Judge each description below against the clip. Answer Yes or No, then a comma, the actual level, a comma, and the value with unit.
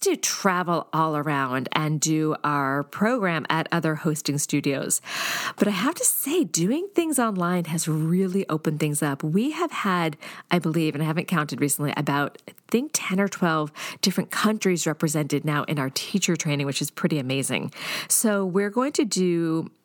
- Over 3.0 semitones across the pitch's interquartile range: Yes, average, 4.7 semitones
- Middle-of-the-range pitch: Yes, medium, 160 Hz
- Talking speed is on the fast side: No, average, 180 wpm